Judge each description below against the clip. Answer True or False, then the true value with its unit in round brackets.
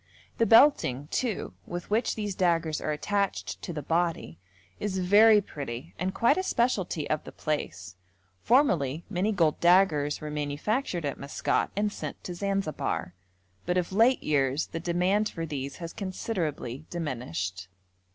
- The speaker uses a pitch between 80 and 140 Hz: False (170 Hz)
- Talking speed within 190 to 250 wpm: False (150 wpm)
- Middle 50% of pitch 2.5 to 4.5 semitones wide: False (5.6 semitones)